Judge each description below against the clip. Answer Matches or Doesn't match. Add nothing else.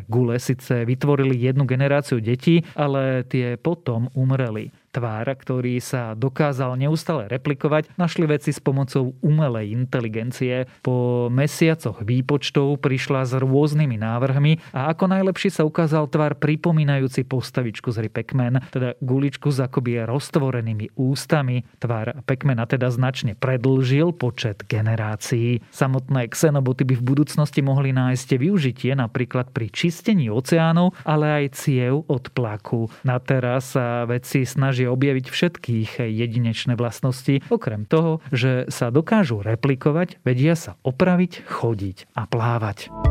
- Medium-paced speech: Matches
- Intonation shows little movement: Doesn't match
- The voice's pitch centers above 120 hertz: Matches